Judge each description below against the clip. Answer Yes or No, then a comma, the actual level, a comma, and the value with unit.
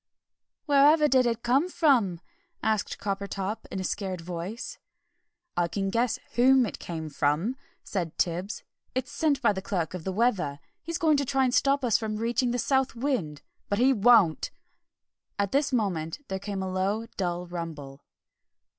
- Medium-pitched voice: No, high, 210 Hz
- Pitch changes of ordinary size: No, wide, 6.0 semitones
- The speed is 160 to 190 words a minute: Yes, average, 165 wpm